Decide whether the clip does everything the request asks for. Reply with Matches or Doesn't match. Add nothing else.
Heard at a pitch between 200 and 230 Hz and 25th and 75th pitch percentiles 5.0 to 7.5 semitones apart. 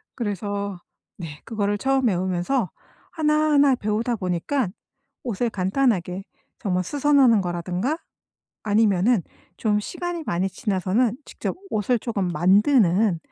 Matches